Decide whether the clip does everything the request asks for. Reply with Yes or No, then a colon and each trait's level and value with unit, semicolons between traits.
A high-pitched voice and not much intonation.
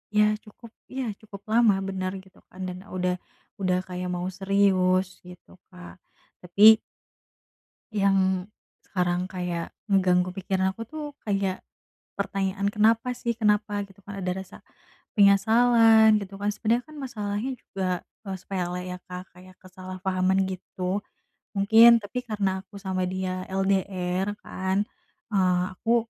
Yes: high, 195 Hz; narrow, 2.1 semitones